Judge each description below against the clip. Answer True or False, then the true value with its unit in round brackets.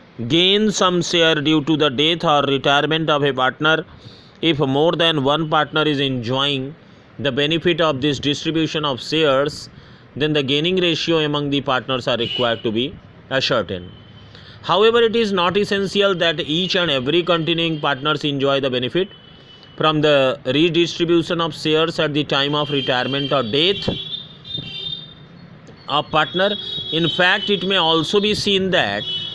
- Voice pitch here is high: False (155 Hz)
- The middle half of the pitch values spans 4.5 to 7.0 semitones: False (3.3 semitones)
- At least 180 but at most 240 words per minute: False (150 wpm)